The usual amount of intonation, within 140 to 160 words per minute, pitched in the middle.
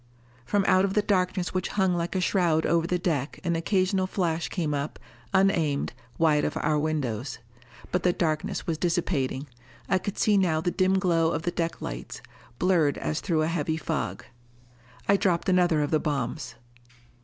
No: average, 3.1 semitones; average, 180 wpm; medium, 170 Hz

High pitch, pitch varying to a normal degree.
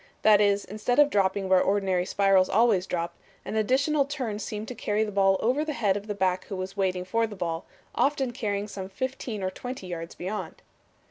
Yes: high, 205 Hz; average, 3.4 semitones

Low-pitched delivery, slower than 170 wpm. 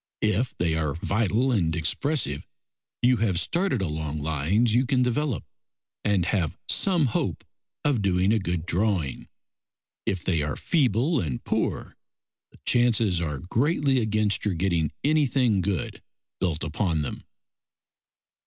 Yes: low, 100 Hz; slow, 135 wpm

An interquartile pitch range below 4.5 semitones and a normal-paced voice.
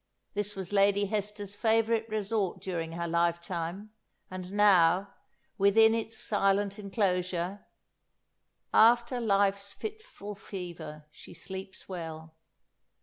No: narrow, 2.6 semitones; slow, 105 wpm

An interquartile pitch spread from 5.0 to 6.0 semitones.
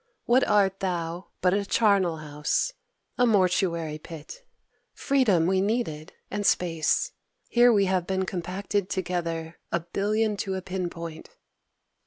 No: average, 3.3 semitones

